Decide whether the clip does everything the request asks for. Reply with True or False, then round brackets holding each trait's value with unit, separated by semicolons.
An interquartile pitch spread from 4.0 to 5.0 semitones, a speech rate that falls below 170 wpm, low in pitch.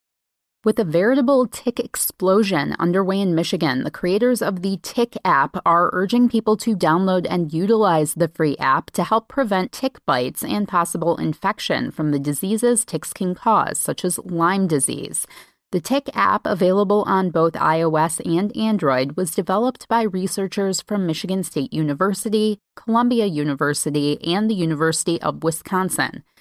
False (4.7 semitones; 150 wpm; 190 Hz)